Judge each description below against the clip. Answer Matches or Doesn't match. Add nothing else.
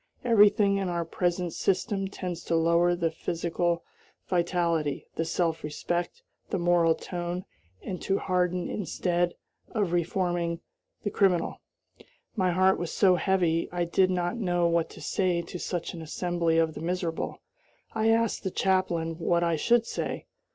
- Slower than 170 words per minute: Matches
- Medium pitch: Matches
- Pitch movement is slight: Matches